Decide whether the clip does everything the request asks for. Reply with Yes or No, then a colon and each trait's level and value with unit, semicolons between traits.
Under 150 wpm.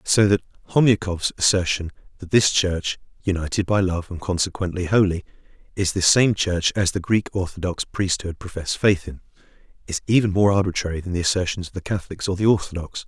No: average, 175 wpm